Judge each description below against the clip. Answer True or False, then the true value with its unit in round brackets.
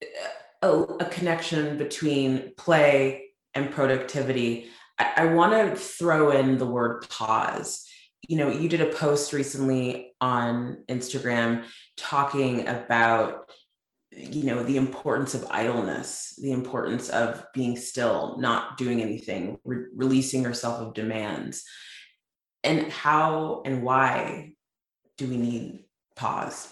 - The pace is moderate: False (120 wpm)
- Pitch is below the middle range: True (130 Hz)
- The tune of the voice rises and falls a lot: False (3.7 semitones)